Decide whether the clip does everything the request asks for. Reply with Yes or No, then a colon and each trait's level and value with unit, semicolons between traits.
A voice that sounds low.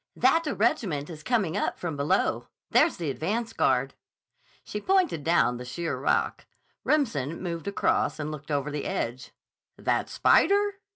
No: medium, 170 Hz